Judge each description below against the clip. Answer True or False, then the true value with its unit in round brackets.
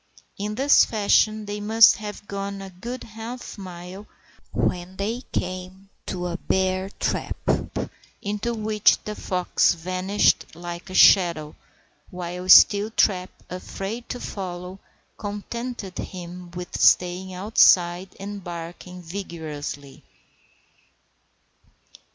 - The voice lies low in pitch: False (190 Hz)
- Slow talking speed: True (105 wpm)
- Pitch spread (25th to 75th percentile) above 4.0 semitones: False (2.7 semitones)